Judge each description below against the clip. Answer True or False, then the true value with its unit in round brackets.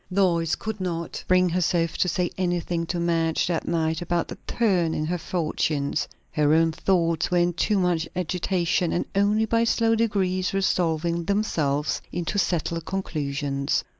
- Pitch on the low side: False (175 Hz)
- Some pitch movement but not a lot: False (2.3 semitones)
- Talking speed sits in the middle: True (155 wpm)